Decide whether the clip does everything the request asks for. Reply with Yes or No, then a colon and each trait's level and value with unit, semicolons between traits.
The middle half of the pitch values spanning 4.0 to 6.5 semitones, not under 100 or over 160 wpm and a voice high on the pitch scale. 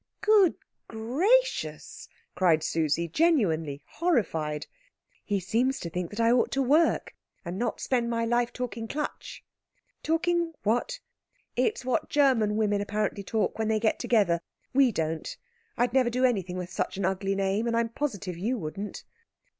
Yes: average, 5.3 semitones; average, 155 wpm; high, 225 Hz